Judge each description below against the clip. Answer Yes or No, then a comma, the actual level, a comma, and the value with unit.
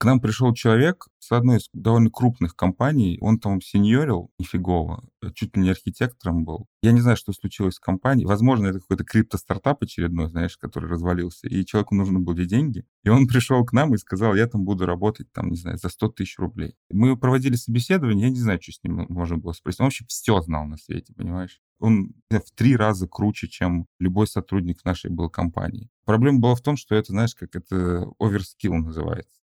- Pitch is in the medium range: No, low, 105 Hz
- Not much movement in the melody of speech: No, average, 4.9 semitones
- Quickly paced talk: Yes, fast, 205 wpm